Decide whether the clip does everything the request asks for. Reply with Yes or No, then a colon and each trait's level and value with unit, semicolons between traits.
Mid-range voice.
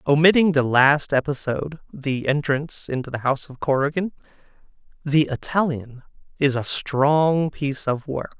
Yes: medium, 145 Hz